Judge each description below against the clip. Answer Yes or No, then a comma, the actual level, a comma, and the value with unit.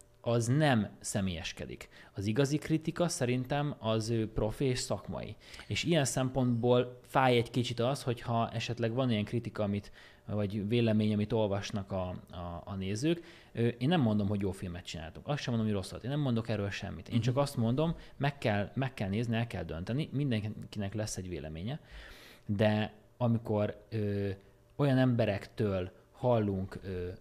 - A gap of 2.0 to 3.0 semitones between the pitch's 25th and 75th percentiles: No, average, 3.6 semitones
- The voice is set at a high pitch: No, low, 115 Hz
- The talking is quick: Yes, fast, 160 wpm